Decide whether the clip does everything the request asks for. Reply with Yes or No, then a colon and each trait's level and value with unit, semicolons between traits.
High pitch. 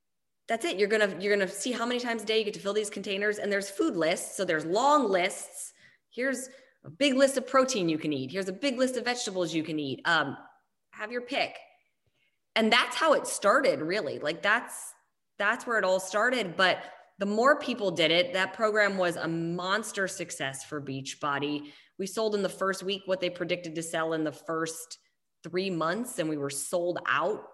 Yes: high, 195 Hz